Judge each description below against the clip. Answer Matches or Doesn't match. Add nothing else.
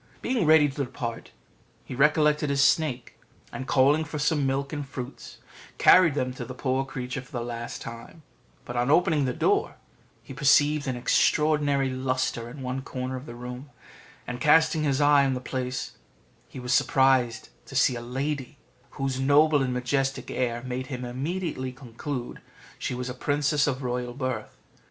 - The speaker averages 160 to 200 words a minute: Matches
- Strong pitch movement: Doesn't match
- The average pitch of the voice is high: Doesn't match